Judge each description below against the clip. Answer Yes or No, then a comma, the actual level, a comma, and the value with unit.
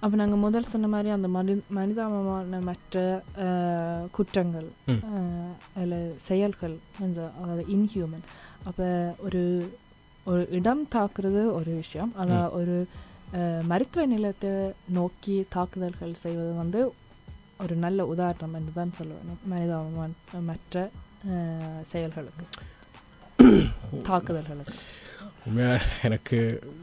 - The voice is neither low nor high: Yes, medium, 180 Hz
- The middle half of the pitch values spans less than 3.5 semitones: Yes, average, 2.8 semitones